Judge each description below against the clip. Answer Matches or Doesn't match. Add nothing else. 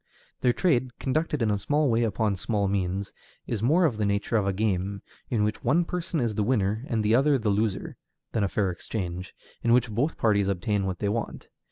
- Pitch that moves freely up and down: Doesn't match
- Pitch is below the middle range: Matches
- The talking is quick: Matches